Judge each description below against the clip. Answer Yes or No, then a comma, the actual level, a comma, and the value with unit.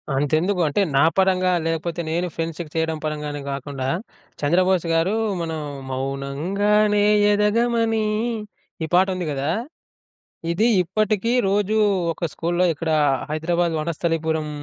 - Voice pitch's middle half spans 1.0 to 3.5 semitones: No, average, 4.0 semitones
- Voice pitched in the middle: Yes, medium, 170 Hz